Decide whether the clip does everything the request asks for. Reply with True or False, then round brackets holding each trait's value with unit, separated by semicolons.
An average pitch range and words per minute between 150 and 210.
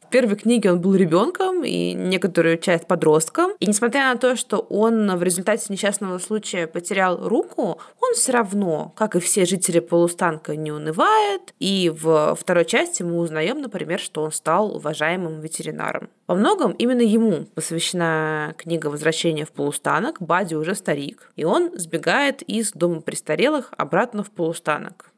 True (4.9 semitones; 155 wpm)